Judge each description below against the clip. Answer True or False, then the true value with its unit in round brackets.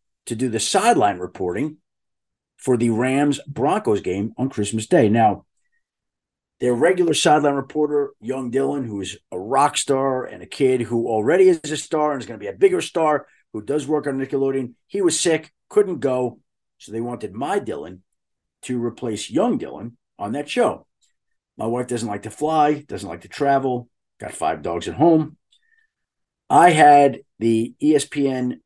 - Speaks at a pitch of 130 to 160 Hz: True (135 Hz)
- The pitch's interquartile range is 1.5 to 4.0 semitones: False (4.5 semitones)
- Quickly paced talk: False (170 wpm)